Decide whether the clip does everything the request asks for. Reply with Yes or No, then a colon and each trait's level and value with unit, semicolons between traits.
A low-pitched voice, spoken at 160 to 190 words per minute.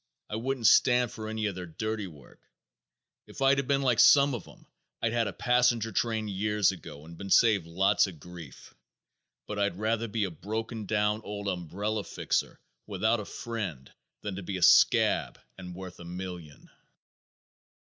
Yes: low, 105 Hz; average, 170 wpm